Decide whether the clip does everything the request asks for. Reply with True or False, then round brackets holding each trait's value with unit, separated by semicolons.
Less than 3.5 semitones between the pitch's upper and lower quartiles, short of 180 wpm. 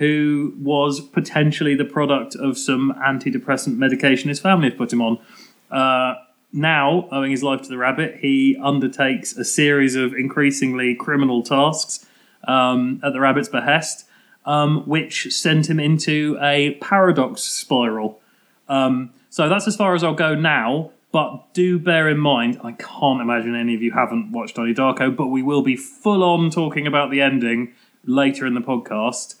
True (2.7 semitones; 165 wpm)